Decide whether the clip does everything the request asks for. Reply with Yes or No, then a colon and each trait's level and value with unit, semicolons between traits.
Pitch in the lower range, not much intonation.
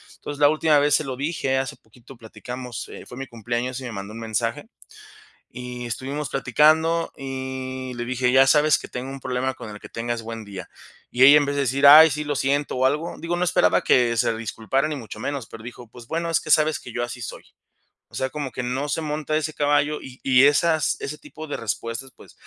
No: low, 130 Hz; average, 3.4 semitones